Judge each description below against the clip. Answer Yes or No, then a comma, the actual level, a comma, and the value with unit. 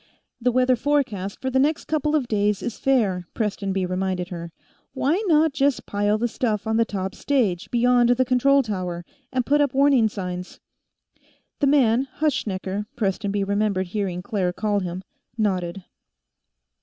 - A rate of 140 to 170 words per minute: Yes, average, 155 wpm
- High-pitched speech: Yes, high, 215 Hz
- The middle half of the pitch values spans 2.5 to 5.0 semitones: No, wide, 5.5 semitones